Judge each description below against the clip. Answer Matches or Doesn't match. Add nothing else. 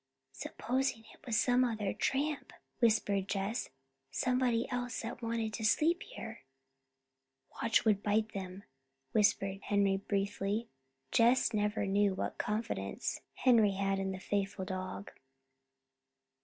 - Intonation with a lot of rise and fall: Doesn't match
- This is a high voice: Matches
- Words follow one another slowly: Matches